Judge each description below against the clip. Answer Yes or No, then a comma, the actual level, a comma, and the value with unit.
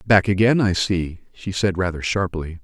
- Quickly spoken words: No, average, 180 wpm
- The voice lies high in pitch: No, very low, 95 Hz